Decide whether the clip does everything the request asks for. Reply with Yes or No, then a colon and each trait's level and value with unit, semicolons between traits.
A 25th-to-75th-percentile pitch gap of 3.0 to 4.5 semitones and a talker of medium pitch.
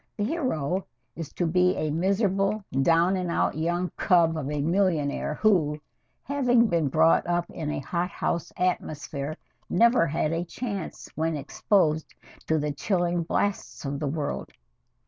Yes: average, 3.7 semitones; medium, 170 Hz